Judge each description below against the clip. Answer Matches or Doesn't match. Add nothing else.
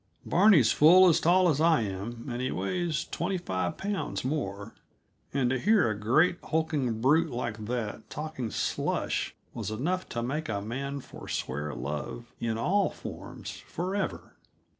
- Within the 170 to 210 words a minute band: Doesn't match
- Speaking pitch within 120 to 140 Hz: Matches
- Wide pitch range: Matches